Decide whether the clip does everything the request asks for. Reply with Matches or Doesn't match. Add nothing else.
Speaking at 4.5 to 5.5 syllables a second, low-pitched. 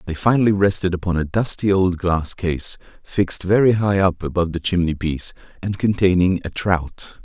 Matches